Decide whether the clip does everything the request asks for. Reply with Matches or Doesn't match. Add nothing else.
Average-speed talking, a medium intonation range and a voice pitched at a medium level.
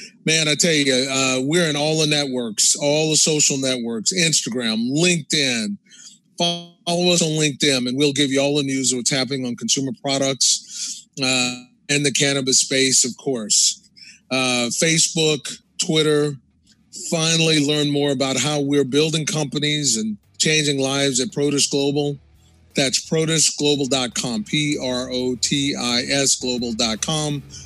Matches